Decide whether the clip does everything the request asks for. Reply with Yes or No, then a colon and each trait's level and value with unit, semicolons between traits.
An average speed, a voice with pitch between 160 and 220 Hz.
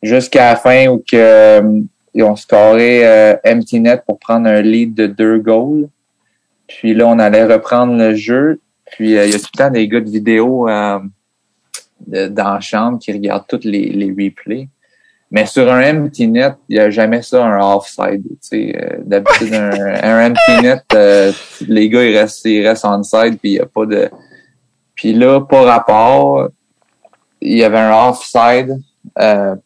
No: average, 185 wpm; low, 110 Hz